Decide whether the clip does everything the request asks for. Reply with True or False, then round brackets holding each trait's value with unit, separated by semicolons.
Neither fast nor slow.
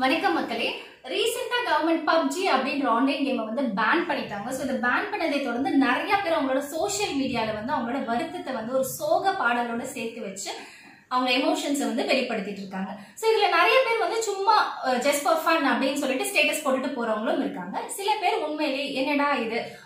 False (155 wpm)